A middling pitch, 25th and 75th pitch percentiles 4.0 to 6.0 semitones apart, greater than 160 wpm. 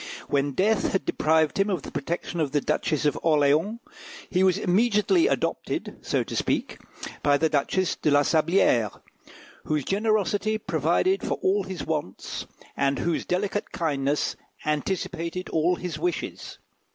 No: medium, 170 Hz; average, 4.7 semitones; average, 145 wpm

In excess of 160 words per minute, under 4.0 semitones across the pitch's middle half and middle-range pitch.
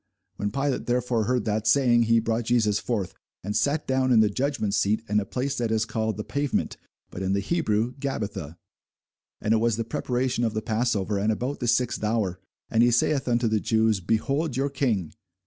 No: average, 200 wpm; average, 2.9 semitones; low, 115 Hz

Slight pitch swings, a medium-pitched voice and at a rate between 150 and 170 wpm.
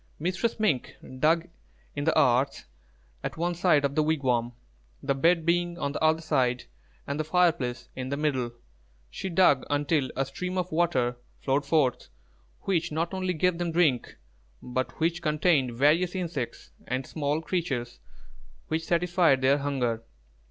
No: average, 4.5 semitones; medium, 155 Hz; average, 155 wpm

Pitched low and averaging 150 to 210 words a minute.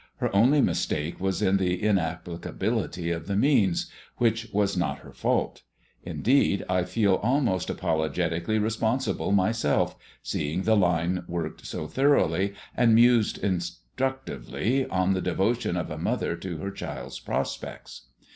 No: very low, 95 Hz; slow, 135 wpm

